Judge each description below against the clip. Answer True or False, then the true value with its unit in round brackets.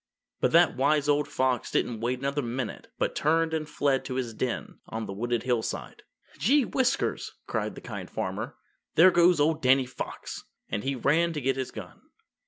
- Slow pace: False (185 wpm)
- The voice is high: False (135 Hz)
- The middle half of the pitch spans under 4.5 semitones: True (3.7 semitones)